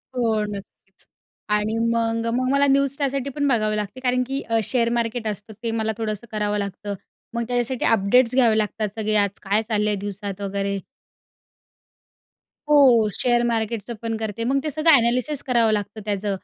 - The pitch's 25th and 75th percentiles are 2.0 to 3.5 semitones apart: Yes, average, 3.1 semitones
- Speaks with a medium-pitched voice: No, high, 225 Hz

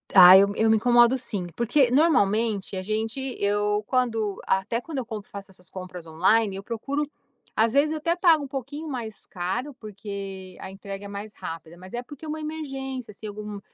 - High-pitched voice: Yes, high, 220 Hz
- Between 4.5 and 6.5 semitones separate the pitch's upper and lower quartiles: Yes, average, 5.0 semitones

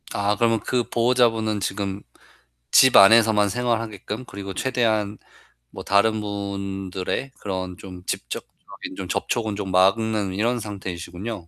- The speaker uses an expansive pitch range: No, average, 2.7 semitones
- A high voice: No, low, 105 Hz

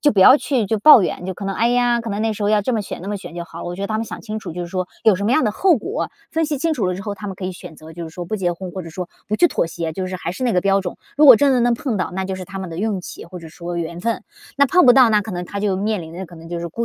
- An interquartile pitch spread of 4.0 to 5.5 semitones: Yes, average, 4.4 semitones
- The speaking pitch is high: Yes, high, 195 Hz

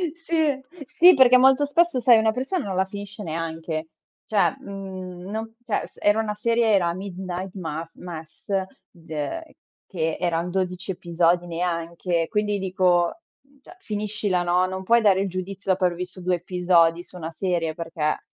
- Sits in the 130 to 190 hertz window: Yes, medium, 185 Hz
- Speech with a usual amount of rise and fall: Yes, average, 3.7 semitones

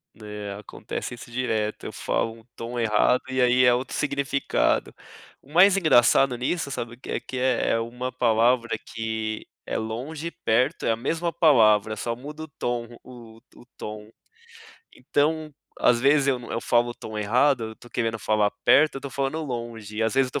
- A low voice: Yes, low, 120 Hz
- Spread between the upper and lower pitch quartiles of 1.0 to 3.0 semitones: No, average, 3.4 semitones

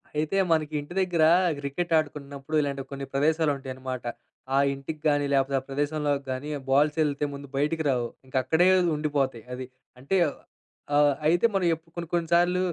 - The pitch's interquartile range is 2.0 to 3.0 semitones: Yes, narrow, 2.6 semitones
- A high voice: No, medium, 145 Hz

